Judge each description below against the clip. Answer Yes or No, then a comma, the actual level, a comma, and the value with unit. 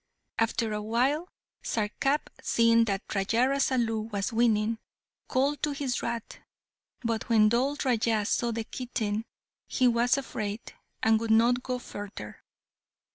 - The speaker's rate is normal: No, slow, 130 wpm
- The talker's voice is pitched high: Yes, high, 230 Hz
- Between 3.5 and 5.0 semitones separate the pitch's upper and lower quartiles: No, narrow, 2.5 semitones